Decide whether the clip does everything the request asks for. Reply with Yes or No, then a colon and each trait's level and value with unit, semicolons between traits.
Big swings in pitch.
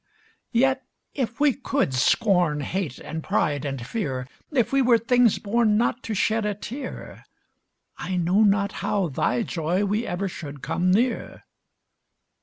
Yes: wide, 6.0 semitones